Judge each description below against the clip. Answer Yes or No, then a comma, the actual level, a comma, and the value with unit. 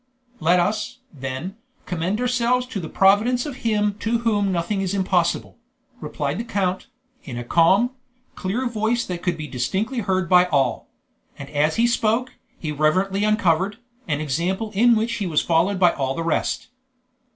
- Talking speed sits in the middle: Yes, average, 165 wpm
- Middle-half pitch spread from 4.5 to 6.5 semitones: Yes, average, 5.0 semitones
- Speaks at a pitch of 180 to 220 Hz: Yes, high, 190 Hz